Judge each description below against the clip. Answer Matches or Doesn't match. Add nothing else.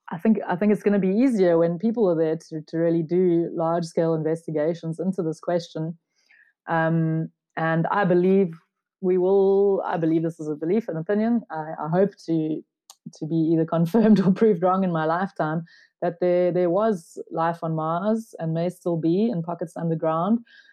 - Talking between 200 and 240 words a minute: Doesn't match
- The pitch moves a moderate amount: Matches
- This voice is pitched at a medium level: Matches